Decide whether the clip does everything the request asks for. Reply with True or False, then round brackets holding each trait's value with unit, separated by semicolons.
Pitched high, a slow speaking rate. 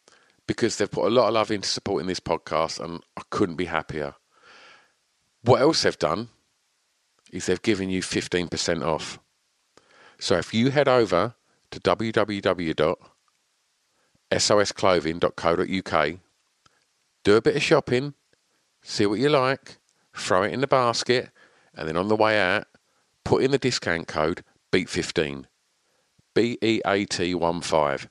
False (95 Hz; 130 wpm)